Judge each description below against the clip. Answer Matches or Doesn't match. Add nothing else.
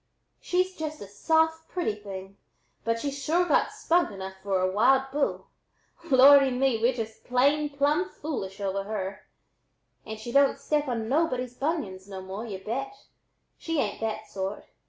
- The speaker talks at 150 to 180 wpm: Matches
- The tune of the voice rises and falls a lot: Matches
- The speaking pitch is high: Matches